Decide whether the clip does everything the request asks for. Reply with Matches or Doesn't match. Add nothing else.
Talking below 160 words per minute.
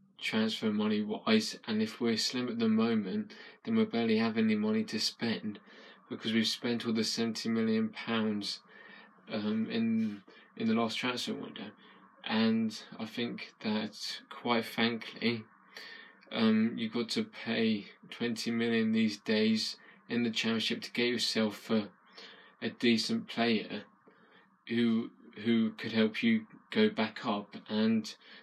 Matches